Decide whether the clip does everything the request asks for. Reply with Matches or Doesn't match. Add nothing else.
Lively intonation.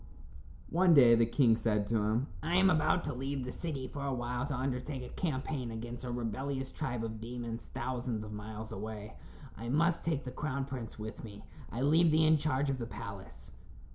Doesn't match